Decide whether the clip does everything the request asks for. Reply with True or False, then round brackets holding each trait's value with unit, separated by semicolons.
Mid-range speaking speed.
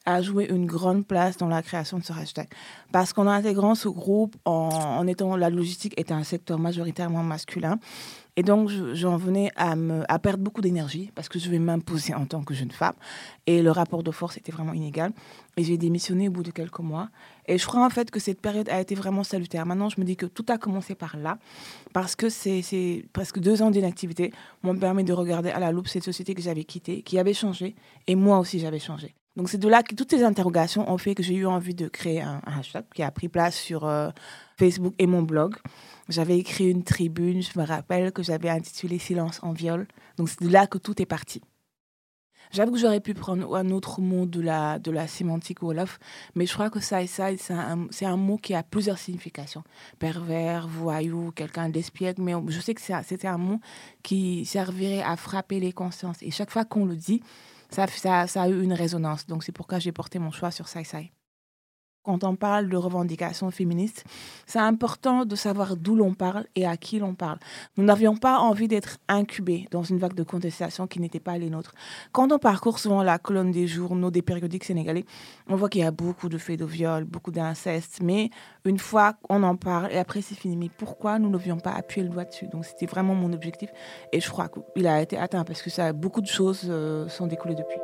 False (225 wpm)